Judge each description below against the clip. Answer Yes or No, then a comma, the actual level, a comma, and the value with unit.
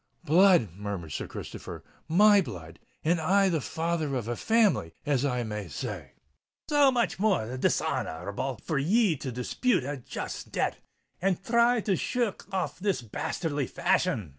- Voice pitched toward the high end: No, medium, 160 Hz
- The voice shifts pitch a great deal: Yes, wide, 8.4 semitones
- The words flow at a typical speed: Yes, average, 170 wpm